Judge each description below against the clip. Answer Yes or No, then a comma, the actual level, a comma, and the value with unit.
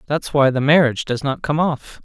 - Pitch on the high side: No, medium, 140 Hz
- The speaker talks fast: Yes, fast, 235 wpm